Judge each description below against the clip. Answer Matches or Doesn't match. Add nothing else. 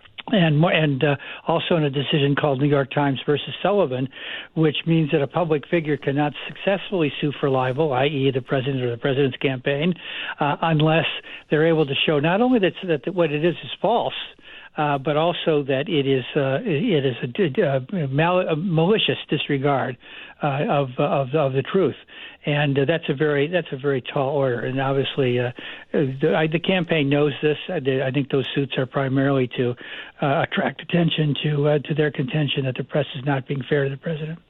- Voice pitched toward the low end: Doesn't match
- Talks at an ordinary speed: Matches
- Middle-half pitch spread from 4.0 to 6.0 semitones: Doesn't match